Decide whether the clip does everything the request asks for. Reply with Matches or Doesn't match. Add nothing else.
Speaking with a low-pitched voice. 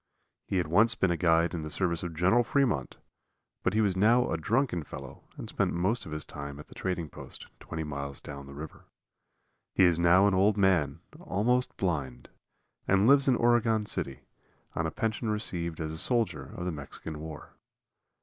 Matches